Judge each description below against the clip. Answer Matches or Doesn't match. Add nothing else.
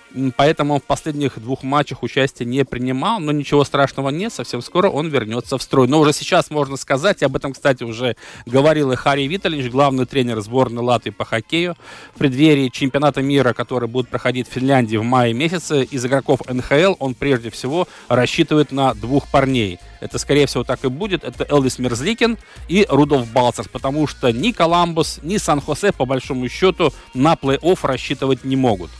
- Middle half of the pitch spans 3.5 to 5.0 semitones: Doesn't match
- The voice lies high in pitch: Doesn't match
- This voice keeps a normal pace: Doesn't match